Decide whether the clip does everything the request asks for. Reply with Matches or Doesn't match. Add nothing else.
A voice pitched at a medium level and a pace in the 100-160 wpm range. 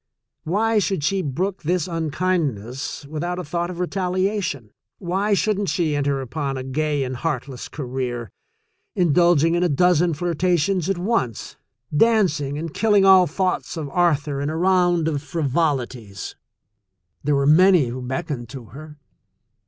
Matches